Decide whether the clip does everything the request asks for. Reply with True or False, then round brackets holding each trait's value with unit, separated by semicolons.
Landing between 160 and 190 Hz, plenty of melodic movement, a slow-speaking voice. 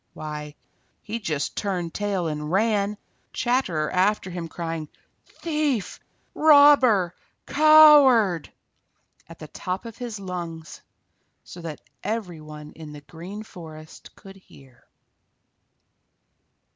True (185 Hz; 5.8 semitones; 105 wpm)